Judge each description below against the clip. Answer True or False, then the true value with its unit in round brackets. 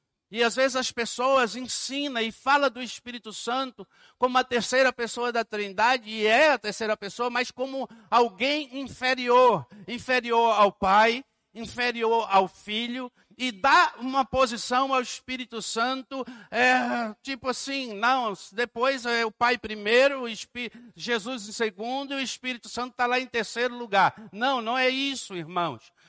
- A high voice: True (240 Hz)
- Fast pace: False (155 wpm)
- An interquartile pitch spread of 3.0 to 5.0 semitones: False (2.6 semitones)